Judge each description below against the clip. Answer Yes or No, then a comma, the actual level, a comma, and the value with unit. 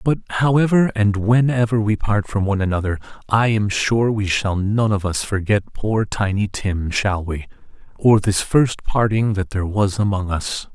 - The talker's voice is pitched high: No, low, 105 Hz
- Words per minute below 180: Yes, average, 170 wpm